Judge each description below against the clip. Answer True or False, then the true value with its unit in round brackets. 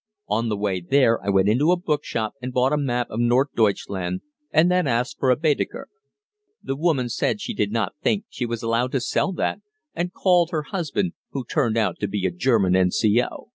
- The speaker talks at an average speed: False (210 wpm)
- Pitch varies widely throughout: True (6.0 semitones)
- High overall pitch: False (125 Hz)